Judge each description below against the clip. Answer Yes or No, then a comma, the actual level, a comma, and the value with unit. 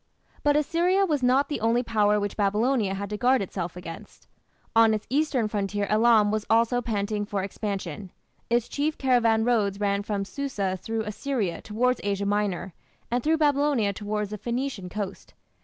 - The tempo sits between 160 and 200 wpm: Yes, average, 165 wpm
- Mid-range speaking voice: No, high, 215 Hz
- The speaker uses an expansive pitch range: No, average, 3.8 semitones